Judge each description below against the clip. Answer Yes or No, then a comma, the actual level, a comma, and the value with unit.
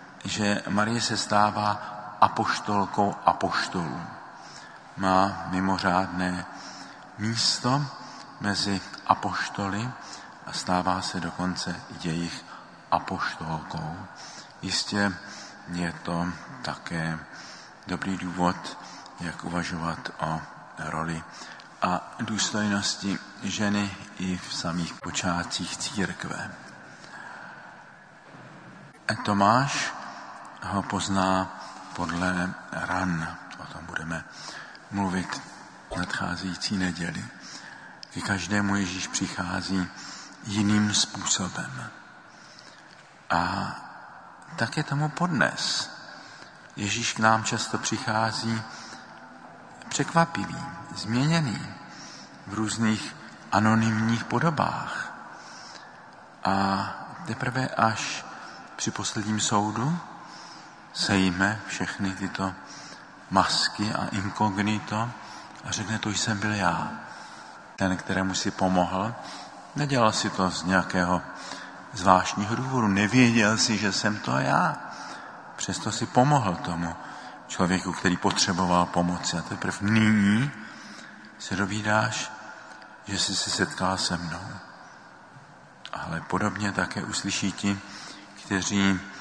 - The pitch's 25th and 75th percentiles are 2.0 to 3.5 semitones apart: Yes, average, 2.9 semitones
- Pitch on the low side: Yes, low, 100 Hz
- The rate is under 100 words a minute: Yes, slow, 85 wpm